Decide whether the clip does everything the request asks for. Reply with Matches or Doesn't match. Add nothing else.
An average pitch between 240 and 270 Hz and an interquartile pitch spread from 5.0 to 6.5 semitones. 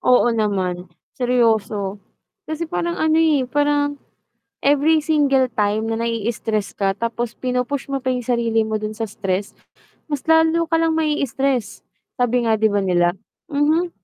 Matches